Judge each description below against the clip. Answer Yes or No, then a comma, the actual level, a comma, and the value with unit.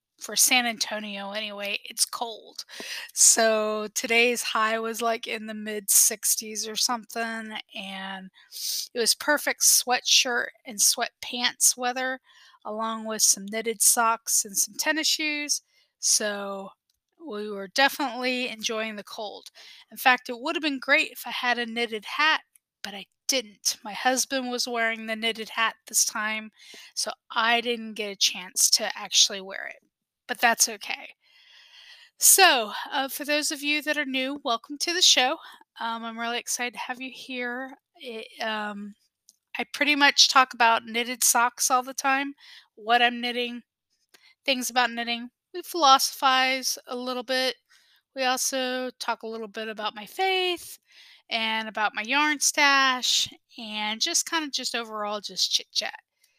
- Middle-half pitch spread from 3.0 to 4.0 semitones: Yes, average, 3.5 semitones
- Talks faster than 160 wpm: No, average, 155 wpm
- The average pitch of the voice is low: No, high, 240 Hz